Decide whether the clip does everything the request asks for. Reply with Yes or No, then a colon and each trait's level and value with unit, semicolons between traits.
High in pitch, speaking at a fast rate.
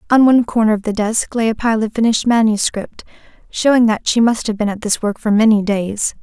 Yes: high, 220 Hz; fast, 230 wpm